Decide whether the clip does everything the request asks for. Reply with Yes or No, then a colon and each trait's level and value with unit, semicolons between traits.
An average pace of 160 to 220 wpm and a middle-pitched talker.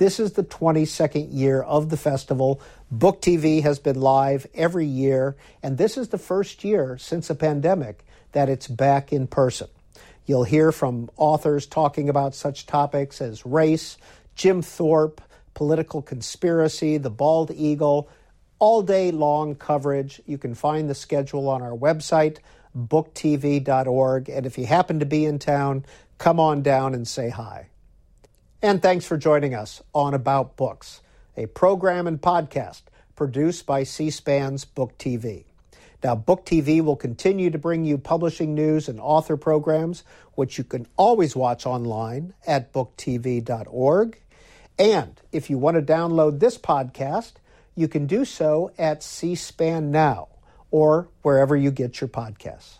No: average, 150 wpm; medium, 145 Hz